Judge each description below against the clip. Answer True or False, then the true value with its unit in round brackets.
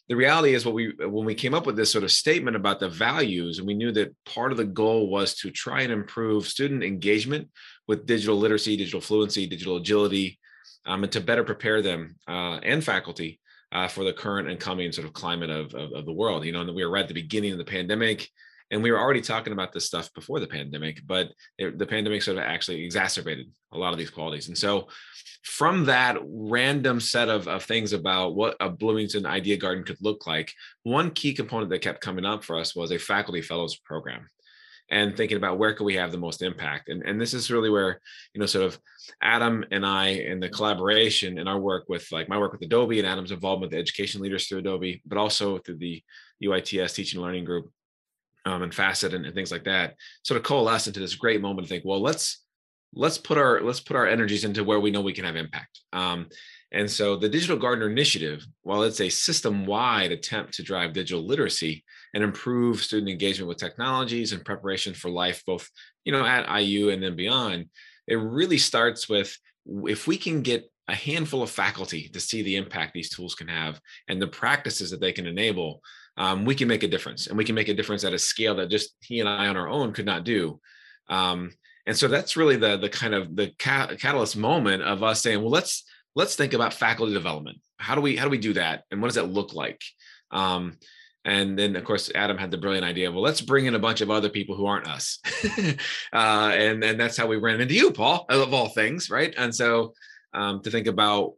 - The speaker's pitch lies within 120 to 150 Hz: False (105 Hz)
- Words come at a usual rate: False (225 wpm)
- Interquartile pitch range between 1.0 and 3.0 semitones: False (3.4 semitones)